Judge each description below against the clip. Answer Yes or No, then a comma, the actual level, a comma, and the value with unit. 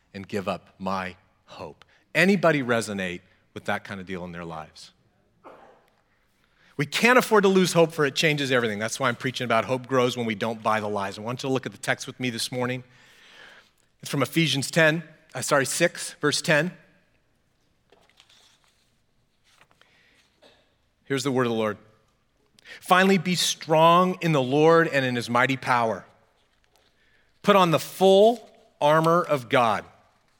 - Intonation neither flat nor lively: No, wide, 6.3 semitones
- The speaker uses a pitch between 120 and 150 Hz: Yes, low, 135 Hz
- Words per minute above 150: Yes, average, 165 wpm